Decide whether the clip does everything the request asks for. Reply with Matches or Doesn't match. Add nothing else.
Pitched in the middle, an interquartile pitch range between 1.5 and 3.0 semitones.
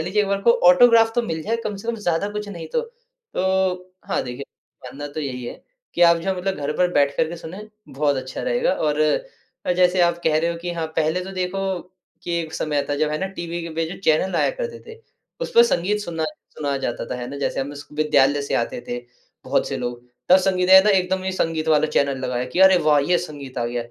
Doesn't match